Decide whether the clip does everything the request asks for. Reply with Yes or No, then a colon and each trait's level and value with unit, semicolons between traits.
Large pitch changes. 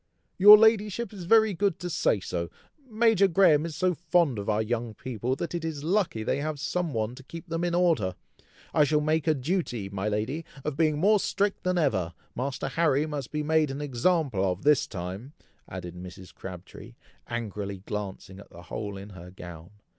Yes: wide, 8.8 semitones